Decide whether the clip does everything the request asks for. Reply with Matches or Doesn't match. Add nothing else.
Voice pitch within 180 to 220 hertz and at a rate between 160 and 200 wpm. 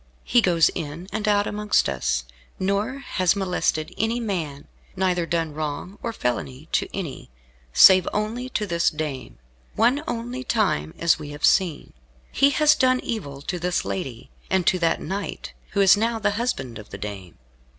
Matches